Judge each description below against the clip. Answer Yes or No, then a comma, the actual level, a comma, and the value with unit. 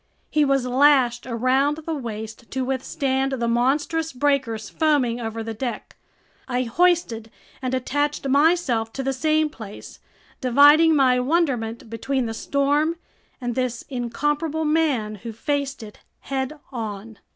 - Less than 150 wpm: Yes, slow, 135 wpm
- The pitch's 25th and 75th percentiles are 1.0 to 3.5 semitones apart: No, average, 3.9 semitones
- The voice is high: Yes, very high, 265 Hz